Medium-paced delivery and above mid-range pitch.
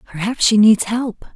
Yes: average, 180 wpm; high, 220 Hz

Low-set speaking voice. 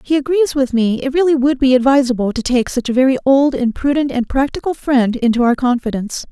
No: very high, 260 Hz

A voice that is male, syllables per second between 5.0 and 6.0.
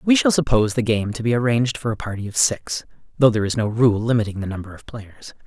No: male; 6.4 syllables/s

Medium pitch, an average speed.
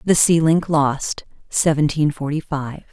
Yes: medium, 150 Hz; average, 145 wpm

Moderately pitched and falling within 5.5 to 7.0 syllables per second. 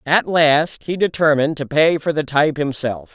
No: medium, 150 Hz; 5.0 syllables/s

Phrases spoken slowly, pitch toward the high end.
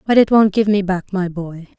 No: fast, 270 wpm; high, 195 Hz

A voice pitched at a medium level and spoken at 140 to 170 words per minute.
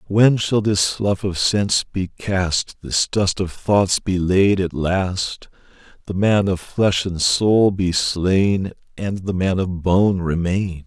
No: very low, 95 Hz; average, 165 wpm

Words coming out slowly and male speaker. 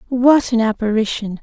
No: slow, 125 wpm; female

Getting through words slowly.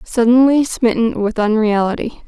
Yes: slow, 105 wpm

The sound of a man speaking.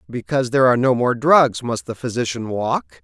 Yes: male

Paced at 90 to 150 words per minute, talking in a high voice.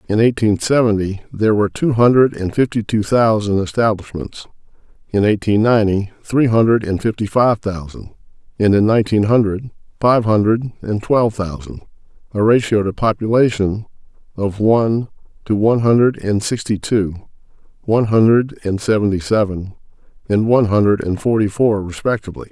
No: average, 145 wpm; low, 110 Hz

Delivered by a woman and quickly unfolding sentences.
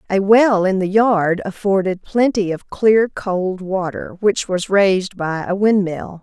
No: female; average, 165 wpm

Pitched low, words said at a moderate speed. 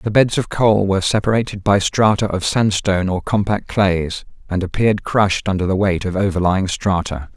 Yes: low, 100 Hz; average, 180 wpm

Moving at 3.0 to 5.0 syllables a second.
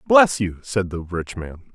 Yes: 4.4 syllables/s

